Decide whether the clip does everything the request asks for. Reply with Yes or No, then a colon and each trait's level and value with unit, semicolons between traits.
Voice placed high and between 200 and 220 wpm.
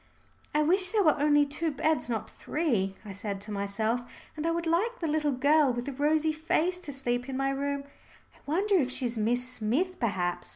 Yes: very high, 285 Hz; fast, 205 wpm